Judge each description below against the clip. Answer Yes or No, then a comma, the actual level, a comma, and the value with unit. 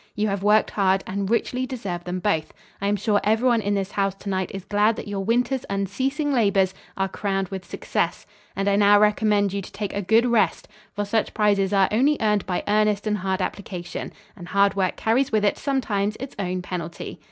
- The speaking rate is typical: No, fast, 210 wpm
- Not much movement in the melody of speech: Yes, narrow, 2.0 semitones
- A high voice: Yes, high, 205 Hz